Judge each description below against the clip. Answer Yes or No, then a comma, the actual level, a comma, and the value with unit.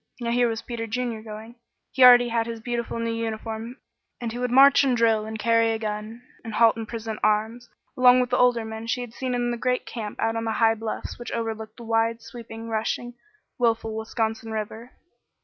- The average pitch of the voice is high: Yes, high, 230 Hz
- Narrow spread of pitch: Yes, narrow, 1.5 semitones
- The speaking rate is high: Yes, fast, 210 wpm